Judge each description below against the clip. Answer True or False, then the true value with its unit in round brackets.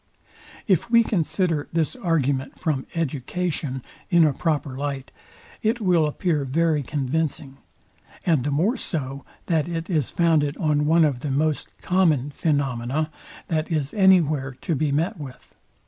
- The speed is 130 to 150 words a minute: True (145 wpm)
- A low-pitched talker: False (155 Hz)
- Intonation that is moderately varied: True (3.1 semitones)